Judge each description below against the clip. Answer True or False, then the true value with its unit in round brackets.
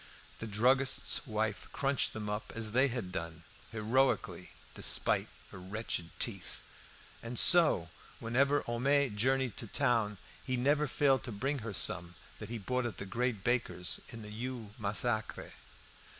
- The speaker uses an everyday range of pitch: True (3.8 semitones)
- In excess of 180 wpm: False (150 wpm)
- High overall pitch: False (115 Hz)